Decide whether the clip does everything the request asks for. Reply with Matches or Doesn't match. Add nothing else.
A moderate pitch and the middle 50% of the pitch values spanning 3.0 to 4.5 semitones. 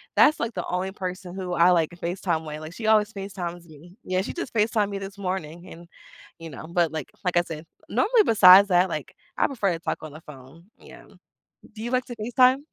Matches